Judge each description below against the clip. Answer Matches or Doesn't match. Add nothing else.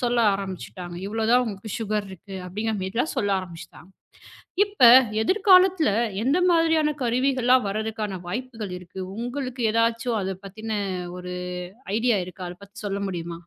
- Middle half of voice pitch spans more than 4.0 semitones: Matches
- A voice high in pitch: Matches